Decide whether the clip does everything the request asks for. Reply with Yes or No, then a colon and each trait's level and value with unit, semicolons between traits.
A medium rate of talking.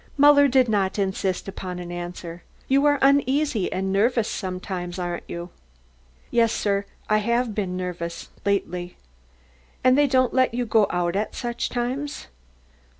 Yes: average, 150 wpm